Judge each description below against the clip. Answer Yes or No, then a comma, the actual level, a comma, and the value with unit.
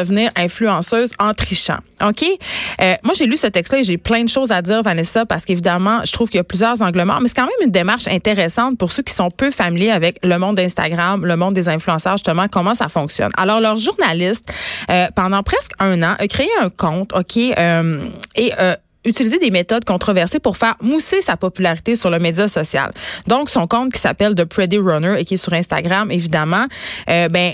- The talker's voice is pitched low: No, high, 195 Hz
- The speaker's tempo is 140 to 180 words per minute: No, average, 215 wpm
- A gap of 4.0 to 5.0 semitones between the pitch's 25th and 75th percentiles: Yes, average, 4.5 semitones